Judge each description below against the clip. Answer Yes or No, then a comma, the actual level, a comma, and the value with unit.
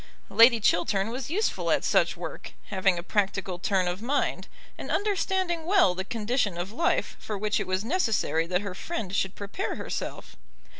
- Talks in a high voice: Yes, high, 210 Hz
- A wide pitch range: Yes, wide, 6.4 semitones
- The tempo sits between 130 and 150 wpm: No, average, 170 wpm